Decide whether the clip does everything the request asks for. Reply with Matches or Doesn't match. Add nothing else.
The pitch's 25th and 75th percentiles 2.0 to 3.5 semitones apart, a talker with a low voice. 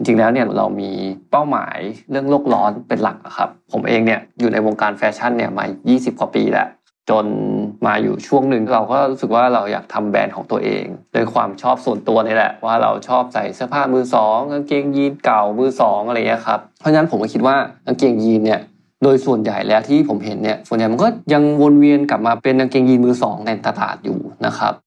Doesn't match